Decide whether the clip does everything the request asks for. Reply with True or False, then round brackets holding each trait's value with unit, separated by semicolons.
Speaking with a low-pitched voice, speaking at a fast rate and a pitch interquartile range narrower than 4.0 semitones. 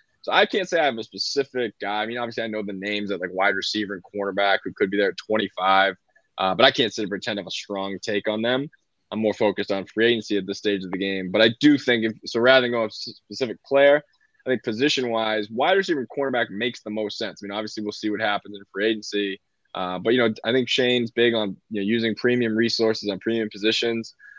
True (110 Hz; 255 wpm; 2.8 semitones)